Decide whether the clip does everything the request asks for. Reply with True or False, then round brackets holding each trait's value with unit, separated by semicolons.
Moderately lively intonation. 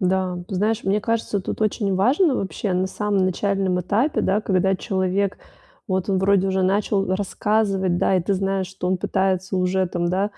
False (1.5 semitones)